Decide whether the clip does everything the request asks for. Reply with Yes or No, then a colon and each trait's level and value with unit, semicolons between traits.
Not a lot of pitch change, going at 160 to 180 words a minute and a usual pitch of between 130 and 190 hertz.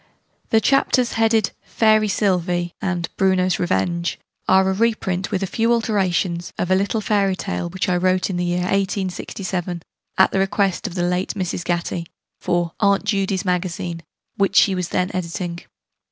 Yes: narrow, 2.1 semitones; average, 165 wpm; medium, 185 Hz